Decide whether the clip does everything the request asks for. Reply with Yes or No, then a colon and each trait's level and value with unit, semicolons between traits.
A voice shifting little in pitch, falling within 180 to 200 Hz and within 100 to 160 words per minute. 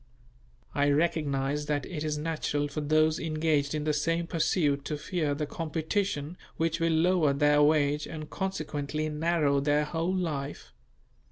No: narrow, 2.0 semitones; medium, 155 Hz; average, 150 wpm